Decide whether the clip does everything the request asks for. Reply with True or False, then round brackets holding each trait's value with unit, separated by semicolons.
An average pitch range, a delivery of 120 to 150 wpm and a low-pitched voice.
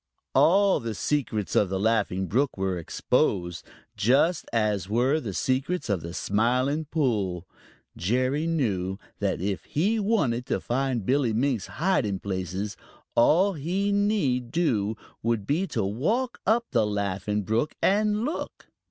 False (7.7 semitones; 140 wpm; 120 Hz)